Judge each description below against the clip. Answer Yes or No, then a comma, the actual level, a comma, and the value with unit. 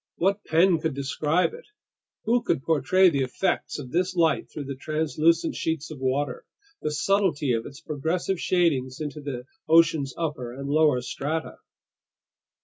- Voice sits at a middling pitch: Yes, medium, 155 Hz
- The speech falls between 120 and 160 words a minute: Yes, average, 150 wpm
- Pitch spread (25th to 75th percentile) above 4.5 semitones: No, average, 3.4 semitones